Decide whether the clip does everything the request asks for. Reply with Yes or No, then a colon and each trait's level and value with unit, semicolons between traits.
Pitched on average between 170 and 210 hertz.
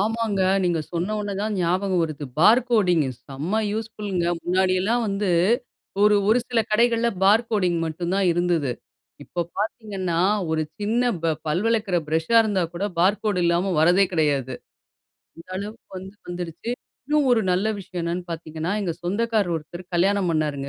Yes: medium, 185 Hz